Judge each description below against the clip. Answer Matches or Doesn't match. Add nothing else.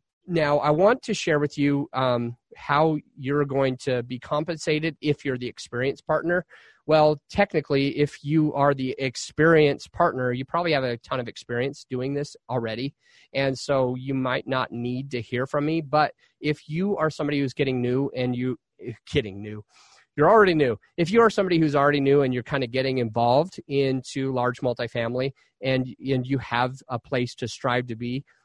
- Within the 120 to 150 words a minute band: Doesn't match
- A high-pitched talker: Doesn't match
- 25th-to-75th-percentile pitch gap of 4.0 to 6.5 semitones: Doesn't match